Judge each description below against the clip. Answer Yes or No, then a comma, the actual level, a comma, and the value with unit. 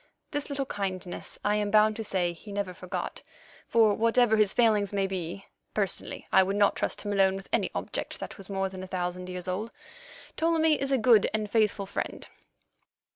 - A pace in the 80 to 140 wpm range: No, average, 190 wpm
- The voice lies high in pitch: Yes, high, 205 Hz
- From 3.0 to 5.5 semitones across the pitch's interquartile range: No, narrow, 2.6 semitones